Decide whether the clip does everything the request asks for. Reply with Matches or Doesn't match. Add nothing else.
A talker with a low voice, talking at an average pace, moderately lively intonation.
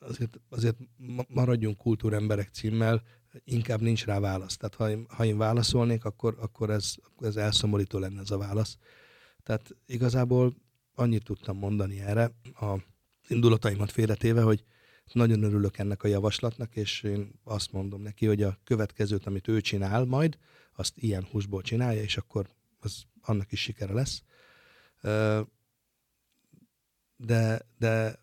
Doesn't match